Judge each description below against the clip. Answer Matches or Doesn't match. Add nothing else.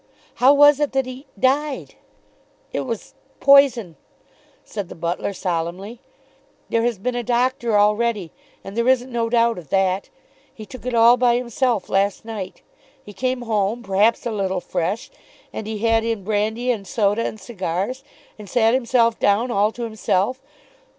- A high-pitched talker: Matches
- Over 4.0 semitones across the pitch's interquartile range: Doesn't match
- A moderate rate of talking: Matches